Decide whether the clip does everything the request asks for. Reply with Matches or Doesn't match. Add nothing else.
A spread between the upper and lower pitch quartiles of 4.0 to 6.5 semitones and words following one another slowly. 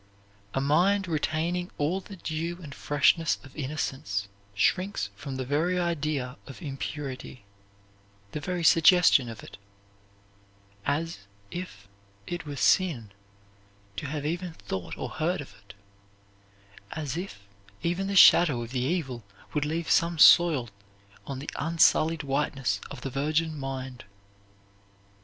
Matches